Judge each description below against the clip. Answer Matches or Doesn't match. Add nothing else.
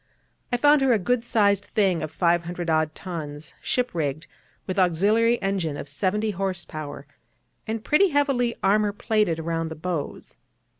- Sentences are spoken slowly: Doesn't match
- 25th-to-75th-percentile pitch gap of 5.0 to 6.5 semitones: Matches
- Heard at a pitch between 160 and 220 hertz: Matches